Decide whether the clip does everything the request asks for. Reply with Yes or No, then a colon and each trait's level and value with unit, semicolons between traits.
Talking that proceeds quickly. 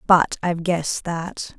No: average, 150 wpm